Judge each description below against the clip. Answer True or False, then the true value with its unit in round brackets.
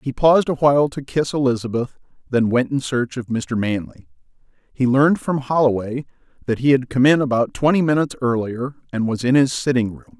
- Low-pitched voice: True (130 Hz)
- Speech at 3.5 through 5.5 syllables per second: False (5.8 syllables/s)